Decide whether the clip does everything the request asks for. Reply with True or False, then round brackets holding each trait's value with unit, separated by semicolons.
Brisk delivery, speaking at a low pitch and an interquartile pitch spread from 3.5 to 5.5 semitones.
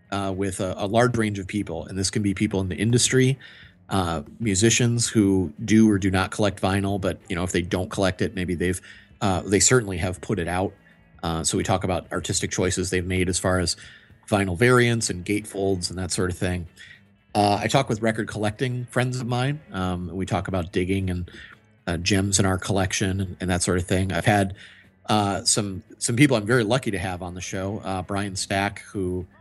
False (215 wpm; 100 Hz; 2.8 semitones)